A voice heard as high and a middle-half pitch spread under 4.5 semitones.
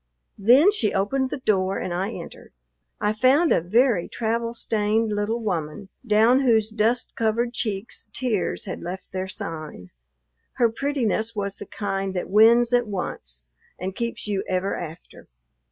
Yes: high, 215 Hz; average, 3.7 semitones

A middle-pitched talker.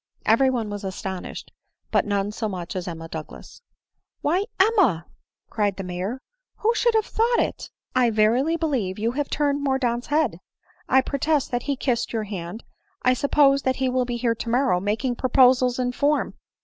No: high, 245 Hz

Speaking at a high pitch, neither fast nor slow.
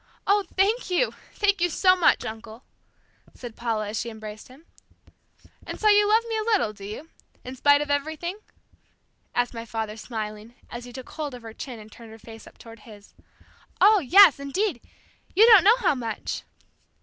Yes: very high, 260 Hz; average, 185 wpm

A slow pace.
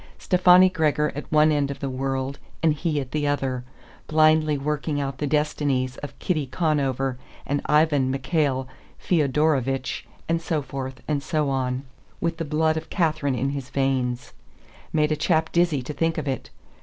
No: average, 170 wpm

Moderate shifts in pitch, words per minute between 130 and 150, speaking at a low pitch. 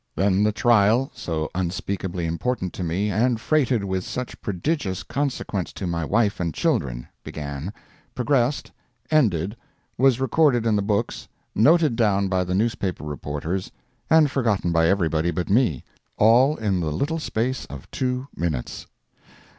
No: wide, 6.3 semitones; average, 140 wpm; low, 100 Hz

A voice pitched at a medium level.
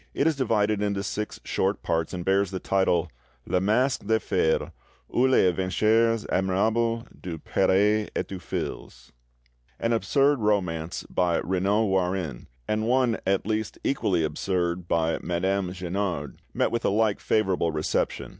No: very low, 95 Hz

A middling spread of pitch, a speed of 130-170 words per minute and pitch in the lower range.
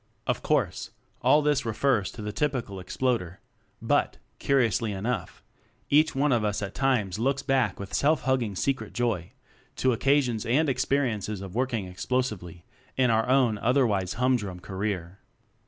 Yes: average, 4.8 semitones; average, 160 wpm; low, 115 Hz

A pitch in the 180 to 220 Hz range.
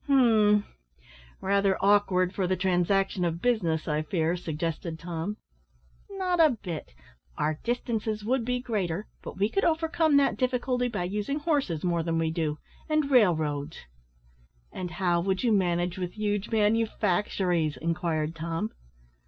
Yes: high, 190 Hz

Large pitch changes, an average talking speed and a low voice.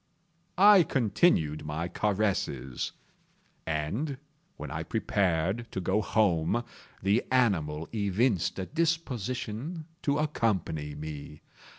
No: wide, 7.9 semitones; slow, 95 wpm; low, 100 Hz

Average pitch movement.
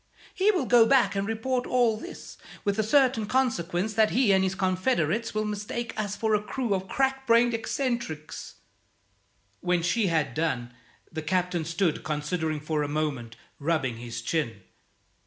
No: wide, 6.7 semitones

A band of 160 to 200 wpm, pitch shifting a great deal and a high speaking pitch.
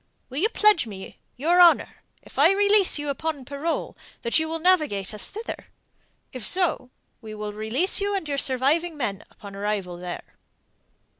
Yes: average, 165 wpm; wide, 8.5 semitones; very high, 285 Hz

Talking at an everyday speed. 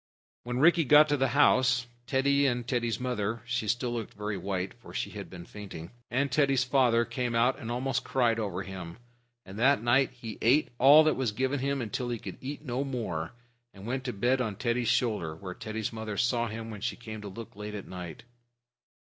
No: fast, 210 wpm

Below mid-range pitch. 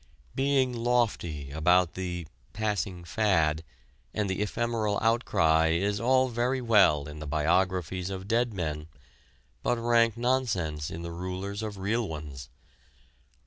Yes: very low, 95 Hz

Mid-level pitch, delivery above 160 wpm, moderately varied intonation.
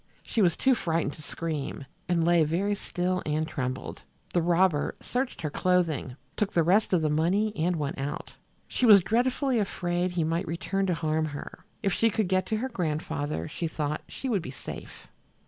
Yes: medium, 175 Hz; average, 190 wpm; average, 4.0 semitones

